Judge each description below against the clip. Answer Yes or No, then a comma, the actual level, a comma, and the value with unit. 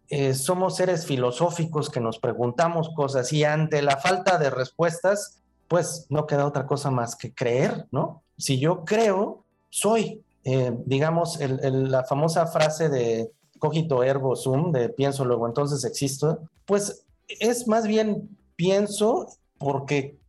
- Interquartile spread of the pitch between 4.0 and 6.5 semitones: Yes, average, 4.5 semitones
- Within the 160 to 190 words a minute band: No, average, 145 wpm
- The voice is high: No, medium, 150 Hz